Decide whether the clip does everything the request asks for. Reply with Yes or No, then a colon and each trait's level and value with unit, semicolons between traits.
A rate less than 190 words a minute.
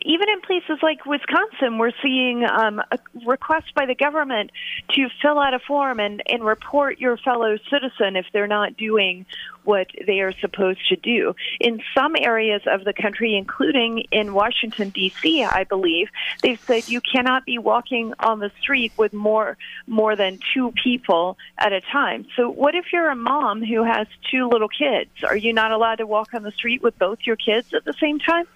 No: average, 195 wpm